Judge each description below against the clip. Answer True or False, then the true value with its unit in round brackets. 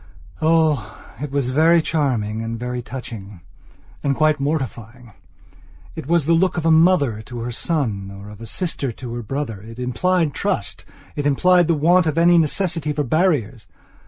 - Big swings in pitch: True (6.0 semitones)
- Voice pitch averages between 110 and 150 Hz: True (140 Hz)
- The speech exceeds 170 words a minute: False (160 wpm)